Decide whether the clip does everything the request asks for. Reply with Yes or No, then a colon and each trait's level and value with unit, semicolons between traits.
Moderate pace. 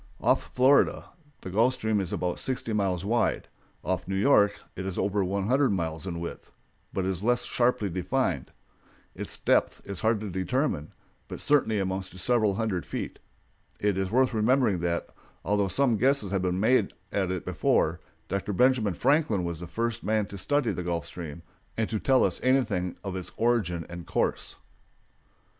Yes: average, 175 wpm